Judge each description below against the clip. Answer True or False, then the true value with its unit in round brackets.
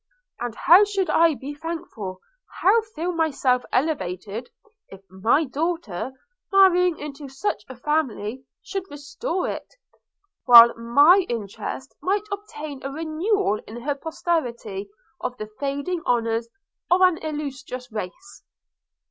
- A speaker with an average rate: False (120 wpm)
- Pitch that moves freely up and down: True (6.5 semitones)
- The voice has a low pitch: False (285 Hz)